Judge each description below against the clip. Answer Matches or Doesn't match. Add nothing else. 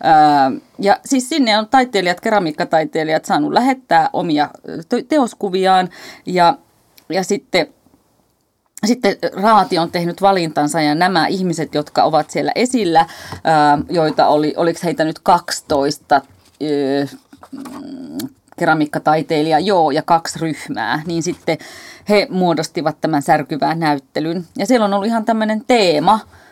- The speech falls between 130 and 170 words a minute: Doesn't match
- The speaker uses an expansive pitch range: Matches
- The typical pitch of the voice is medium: Matches